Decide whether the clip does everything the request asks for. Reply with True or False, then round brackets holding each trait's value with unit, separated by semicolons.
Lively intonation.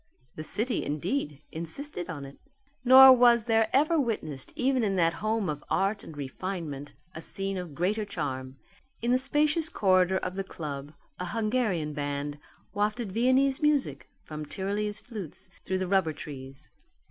True (7.5 semitones)